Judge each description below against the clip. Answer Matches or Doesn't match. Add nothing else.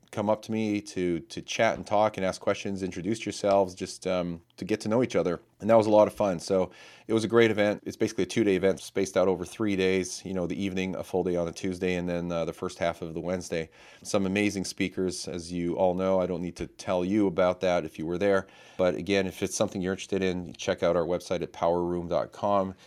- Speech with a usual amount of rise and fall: Doesn't match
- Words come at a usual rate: Doesn't match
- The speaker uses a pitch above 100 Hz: Doesn't match